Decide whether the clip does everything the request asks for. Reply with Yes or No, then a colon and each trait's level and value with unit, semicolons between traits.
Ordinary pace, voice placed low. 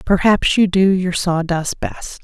No: average, 160 wpm; medium, 185 Hz